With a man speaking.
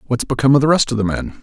Yes: male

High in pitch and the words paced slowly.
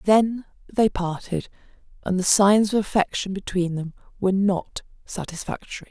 Yes: high, 195 Hz; slow, 130 wpm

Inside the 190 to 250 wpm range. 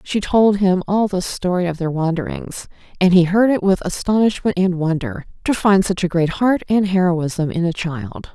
Yes: average, 200 wpm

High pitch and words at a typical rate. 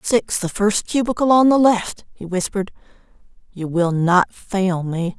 Yes: high, 200 Hz; average, 160 wpm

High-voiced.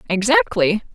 Yes: high, 230 Hz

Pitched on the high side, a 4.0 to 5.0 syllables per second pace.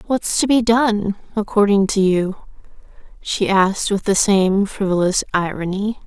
Yes: high, 200 Hz; 4.3 syllables/s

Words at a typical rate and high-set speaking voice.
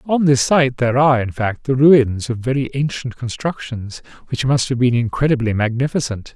No: average, 180 wpm; low, 125 Hz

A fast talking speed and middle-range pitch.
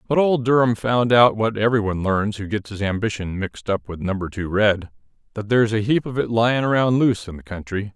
No: fast, 225 wpm; low, 110 Hz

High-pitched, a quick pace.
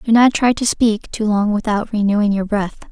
Yes: high, 215 Hz; fast, 225 wpm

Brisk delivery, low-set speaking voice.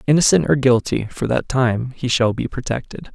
No: average, 190 wpm; low, 130 Hz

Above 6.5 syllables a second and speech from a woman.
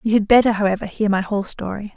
Yes: 7.0 syllables/s; female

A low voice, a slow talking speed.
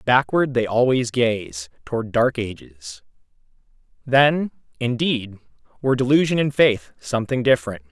Yes: low, 120 Hz; slow, 115 wpm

